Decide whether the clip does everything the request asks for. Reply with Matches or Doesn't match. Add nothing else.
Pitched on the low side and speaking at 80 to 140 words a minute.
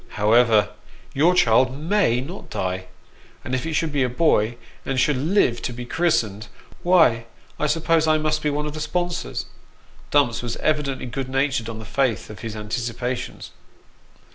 Doesn't match